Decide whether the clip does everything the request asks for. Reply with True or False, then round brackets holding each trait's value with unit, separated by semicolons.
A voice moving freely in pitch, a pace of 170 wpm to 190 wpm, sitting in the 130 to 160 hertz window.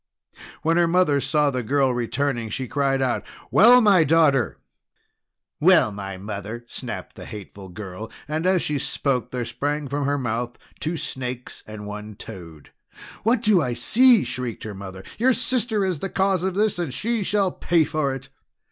True (7.4 semitones; 175 wpm; 140 Hz)